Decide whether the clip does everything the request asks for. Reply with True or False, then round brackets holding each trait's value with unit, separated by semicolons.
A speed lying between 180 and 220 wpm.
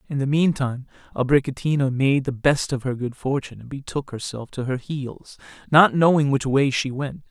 True (190 wpm)